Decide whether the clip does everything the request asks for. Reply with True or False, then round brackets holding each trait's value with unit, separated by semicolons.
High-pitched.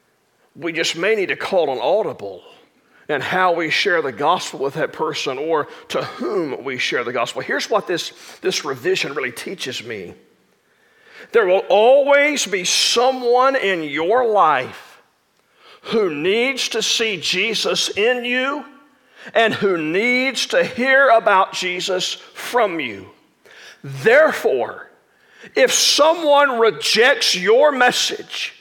True (245 Hz)